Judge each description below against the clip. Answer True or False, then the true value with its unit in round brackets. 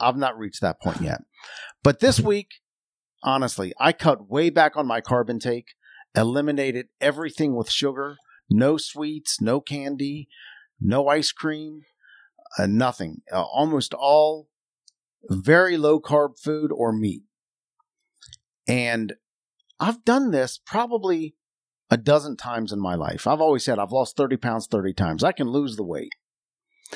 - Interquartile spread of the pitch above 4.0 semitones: True (4.6 semitones)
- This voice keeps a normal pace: True (145 wpm)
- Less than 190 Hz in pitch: True (140 Hz)